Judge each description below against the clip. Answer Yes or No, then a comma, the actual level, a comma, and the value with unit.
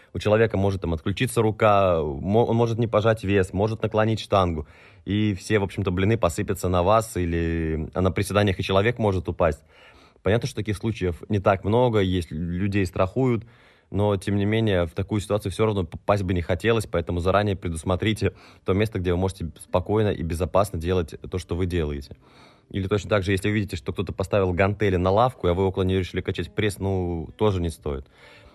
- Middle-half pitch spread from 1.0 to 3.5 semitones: Yes, average, 2.8 semitones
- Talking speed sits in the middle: No, fast, 195 wpm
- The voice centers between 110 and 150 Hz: No, low, 100 Hz